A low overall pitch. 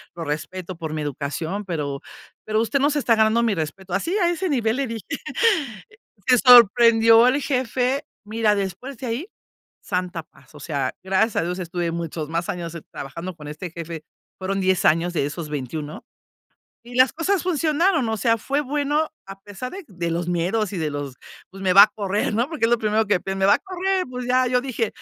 No: high, 205 Hz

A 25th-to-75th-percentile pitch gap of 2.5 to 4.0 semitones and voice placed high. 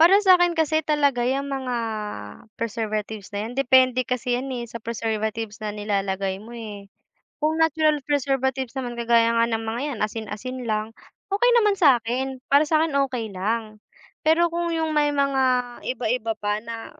No: average, 4.4 semitones; high, 245 Hz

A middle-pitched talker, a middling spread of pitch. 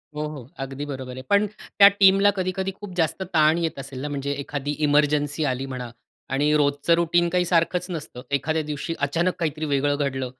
Yes: medium, 150 Hz; average, 3.5 semitones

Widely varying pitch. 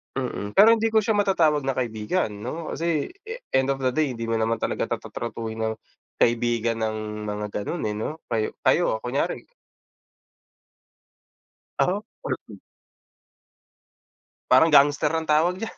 Yes: wide, 6.5 semitones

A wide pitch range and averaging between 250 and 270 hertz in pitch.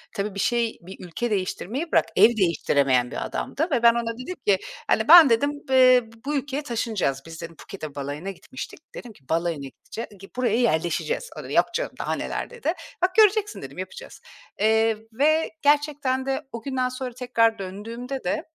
No: wide, 6.3 semitones; high, 235 Hz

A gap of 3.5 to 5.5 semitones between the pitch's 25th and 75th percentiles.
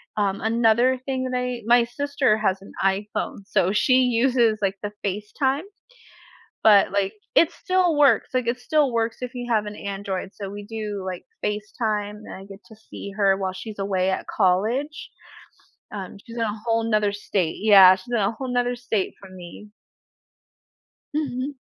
Yes: average, 3.8 semitones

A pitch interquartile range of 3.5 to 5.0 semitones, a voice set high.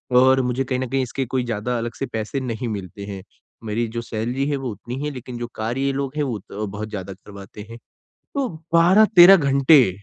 No: average, 4.0 semitones; low, 125 Hz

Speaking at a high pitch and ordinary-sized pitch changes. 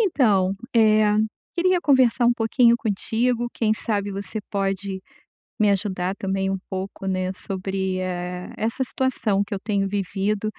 Yes: high, 200 Hz; average, 3.1 semitones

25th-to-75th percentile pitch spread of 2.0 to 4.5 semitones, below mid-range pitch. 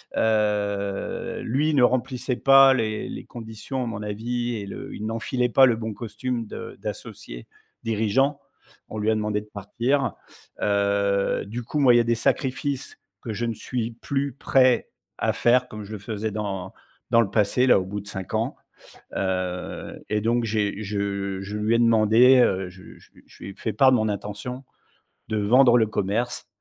Yes: average, 3.1 semitones; low, 110 Hz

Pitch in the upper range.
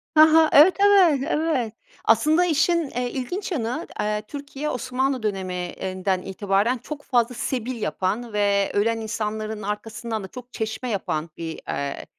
Yes: high, 230 Hz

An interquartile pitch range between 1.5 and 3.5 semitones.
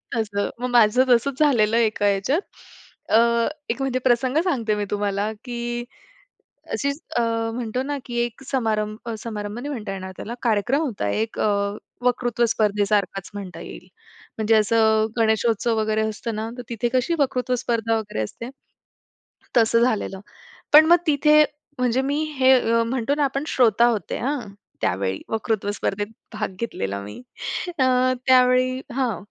Yes: average, 3.2 semitones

